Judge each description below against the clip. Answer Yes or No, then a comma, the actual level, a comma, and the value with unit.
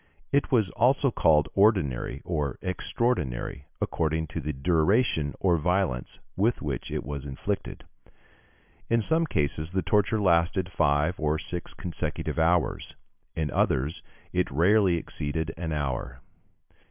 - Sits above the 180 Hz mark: No, very low, 80 Hz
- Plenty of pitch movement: No, average, 4.7 semitones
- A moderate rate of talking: No, slow, 130 wpm